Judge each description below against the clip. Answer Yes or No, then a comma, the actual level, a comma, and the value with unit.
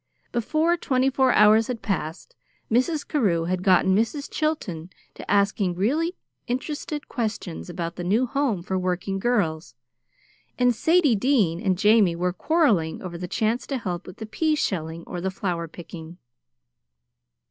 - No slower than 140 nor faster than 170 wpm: Yes, average, 150 wpm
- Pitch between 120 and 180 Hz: No, high, 205 Hz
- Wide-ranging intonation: Yes, wide, 6.5 semitones